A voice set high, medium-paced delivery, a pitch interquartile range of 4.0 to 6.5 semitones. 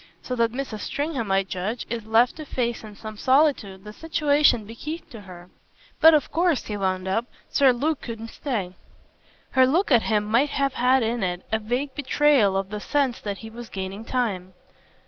Yes: high, 230 Hz; average, 190 wpm; average, 4.9 semitones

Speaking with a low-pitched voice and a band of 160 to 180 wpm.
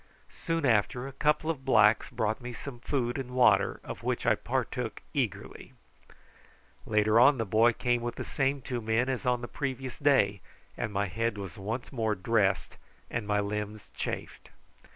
Yes: low, 120 Hz; average, 175 wpm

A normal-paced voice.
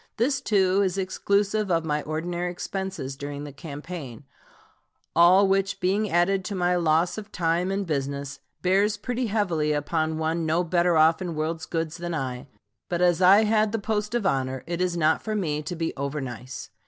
Yes: average, 185 wpm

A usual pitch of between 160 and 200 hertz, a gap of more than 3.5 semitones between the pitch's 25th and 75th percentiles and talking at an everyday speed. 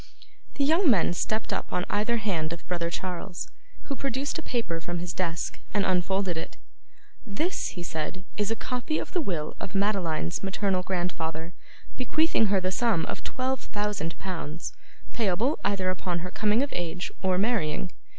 Yes: high, 190 Hz; average, 4.5 semitones; average, 170 wpm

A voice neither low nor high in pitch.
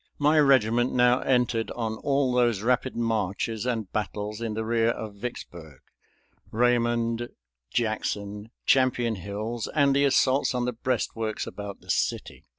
No: low, 115 Hz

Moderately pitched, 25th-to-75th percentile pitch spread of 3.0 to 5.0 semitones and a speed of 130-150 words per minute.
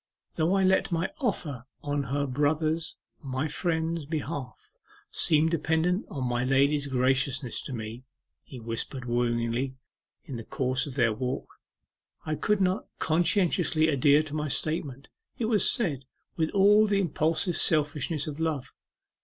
Yes: medium, 150 Hz; average, 4.0 semitones; average, 145 wpm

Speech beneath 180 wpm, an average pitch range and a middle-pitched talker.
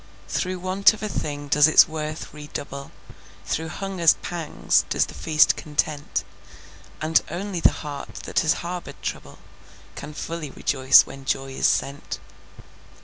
Yes: average, 145 wpm; average, 3.1 semitones; medium, 155 Hz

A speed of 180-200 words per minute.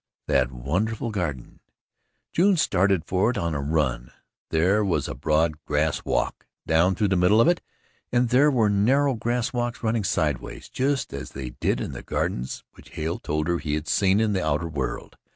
Yes: average, 190 wpm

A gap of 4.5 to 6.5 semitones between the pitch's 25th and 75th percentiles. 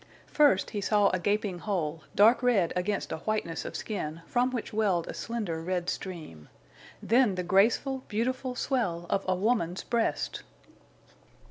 Yes: average, 4.9 semitones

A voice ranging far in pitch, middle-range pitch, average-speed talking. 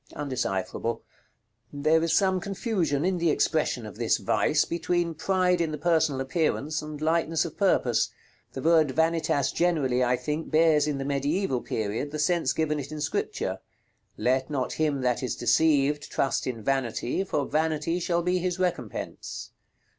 No: average, 3.7 semitones; medium, 155 Hz; average, 160 wpm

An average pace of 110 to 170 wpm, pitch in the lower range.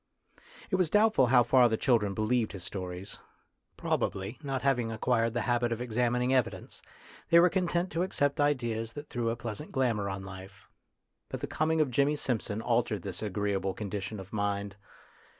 No: average, 185 wpm; low, 120 Hz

